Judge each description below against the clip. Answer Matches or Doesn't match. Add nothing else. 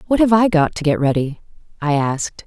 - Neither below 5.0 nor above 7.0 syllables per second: Matches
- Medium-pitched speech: Matches